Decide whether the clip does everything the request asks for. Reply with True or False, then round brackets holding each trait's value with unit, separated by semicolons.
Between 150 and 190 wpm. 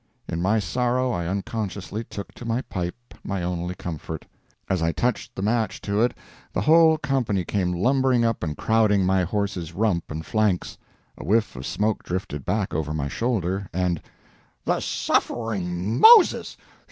True (160 wpm)